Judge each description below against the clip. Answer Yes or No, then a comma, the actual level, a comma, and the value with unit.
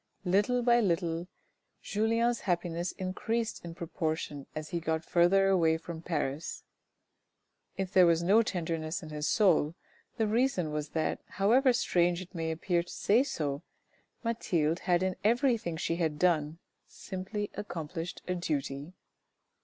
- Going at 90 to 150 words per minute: Yes, average, 140 wpm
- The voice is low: No, medium, 175 Hz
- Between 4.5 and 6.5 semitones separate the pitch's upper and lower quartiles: No, average, 3.9 semitones